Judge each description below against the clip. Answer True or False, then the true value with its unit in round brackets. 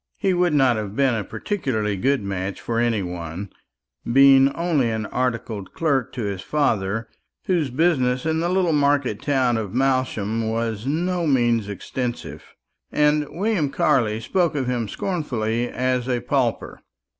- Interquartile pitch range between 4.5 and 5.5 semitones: True (5.0 semitones)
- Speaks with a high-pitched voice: False (125 Hz)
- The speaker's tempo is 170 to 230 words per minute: False (155 wpm)